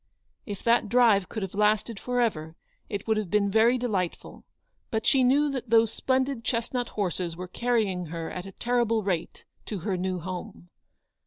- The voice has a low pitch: No, high, 215 Hz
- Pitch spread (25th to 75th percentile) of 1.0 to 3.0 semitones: No, average, 4.4 semitones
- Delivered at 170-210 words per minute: Yes, average, 175 wpm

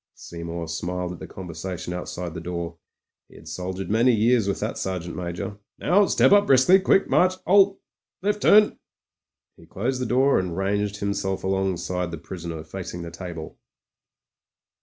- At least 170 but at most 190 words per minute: No, average, 160 wpm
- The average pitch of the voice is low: Yes, very low, 95 Hz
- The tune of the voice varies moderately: No, wide, 6.0 semitones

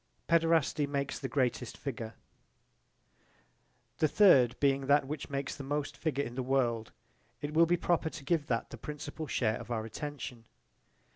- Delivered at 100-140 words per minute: No, average, 160 wpm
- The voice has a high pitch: No, medium, 140 Hz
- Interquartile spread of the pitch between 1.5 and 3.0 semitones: No, average, 3.4 semitones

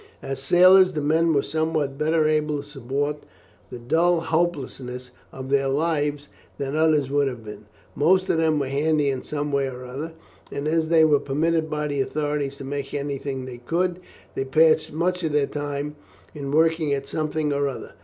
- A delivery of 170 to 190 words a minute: Yes, average, 185 wpm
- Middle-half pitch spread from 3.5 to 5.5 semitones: No, narrow, 2.5 semitones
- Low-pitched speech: No, medium, 145 Hz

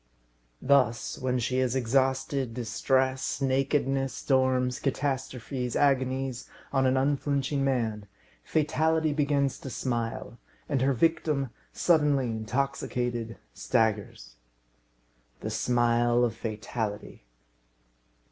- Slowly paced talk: Yes, slow, 90 wpm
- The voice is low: Yes, low, 130 Hz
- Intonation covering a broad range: No, narrow, 2.5 semitones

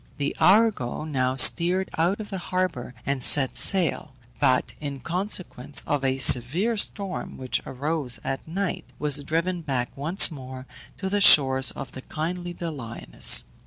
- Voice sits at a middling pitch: Yes, medium, 150 Hz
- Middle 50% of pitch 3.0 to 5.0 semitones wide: No, wide, 5.6 semitones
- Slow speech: No, average, 150 wpm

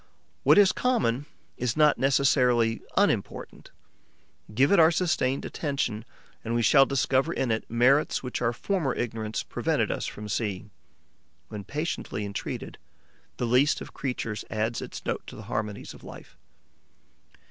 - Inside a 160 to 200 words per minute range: No, average, 145 wpm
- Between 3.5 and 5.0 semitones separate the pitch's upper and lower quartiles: Yes, average, 4.2 semitones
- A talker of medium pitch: No, low, 125 Hz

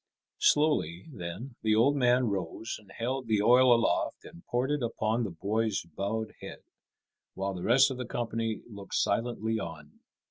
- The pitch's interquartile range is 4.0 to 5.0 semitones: No, average, 3.5 semitones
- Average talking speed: Yes, average, 165 wpm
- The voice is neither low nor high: No, low, 115 Hz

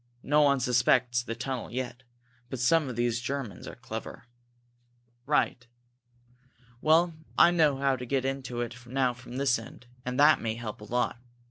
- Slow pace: No, average, 165 wpm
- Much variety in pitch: No, narrow, 2.4 semitones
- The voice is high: No, low, 125 Hz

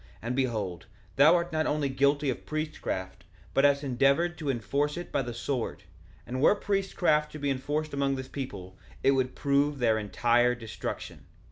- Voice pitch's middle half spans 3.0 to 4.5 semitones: Yes, average, 3.6 semitones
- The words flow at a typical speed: Yes, average, 170 wpm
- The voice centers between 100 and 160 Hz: Yes, medium, 140 Hz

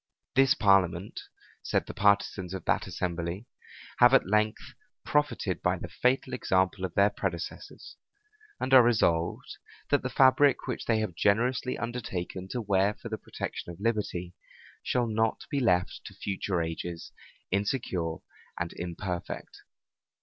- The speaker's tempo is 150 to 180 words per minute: No, average, 140 wpm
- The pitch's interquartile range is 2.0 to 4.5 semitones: No, average, 5.1 semitones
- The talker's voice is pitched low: Yes, low, 100 Hz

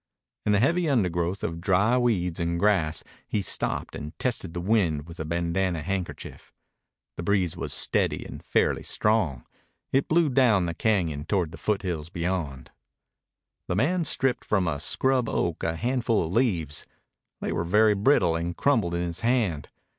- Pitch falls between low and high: No, very low, 90 Hz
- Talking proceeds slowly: No, average, 165 wpm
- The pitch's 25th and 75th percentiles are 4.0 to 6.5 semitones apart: Yes, average, 5.1 semitones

